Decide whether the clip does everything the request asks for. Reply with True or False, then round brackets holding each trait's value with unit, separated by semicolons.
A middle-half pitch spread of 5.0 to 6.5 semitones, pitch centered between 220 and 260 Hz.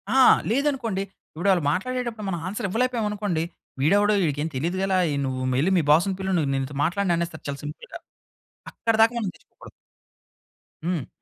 False (5.4 semitones; 190 Hz)